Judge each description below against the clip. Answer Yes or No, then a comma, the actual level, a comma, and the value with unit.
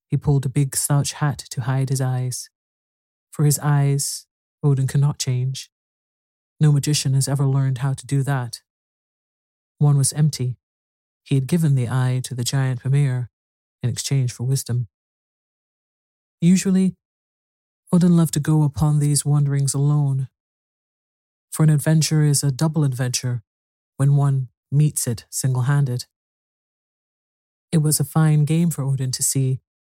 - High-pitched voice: No, low, 135 Hz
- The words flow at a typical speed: Yes, average, 145 wpm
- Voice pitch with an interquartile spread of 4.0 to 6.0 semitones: No, average, 2.8 semitones